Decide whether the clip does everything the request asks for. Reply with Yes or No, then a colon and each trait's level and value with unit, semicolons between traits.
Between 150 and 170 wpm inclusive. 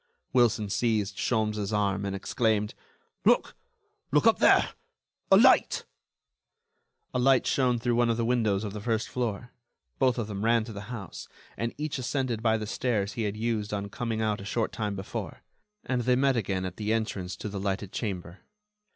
No: average, 185 wpm